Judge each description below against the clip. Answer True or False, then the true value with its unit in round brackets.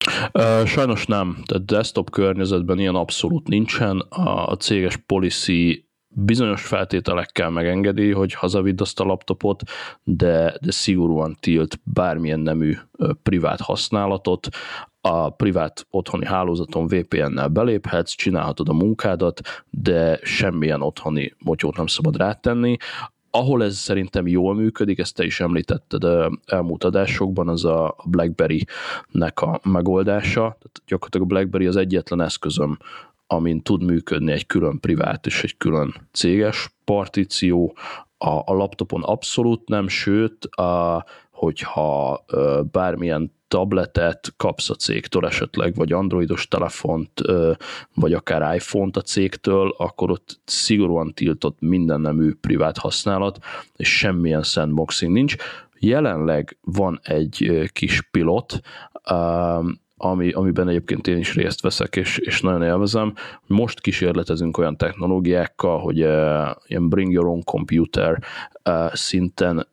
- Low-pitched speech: True (90 Hz)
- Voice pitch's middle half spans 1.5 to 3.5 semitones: True (3.1 semitones)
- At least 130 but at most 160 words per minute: False (120 wpm)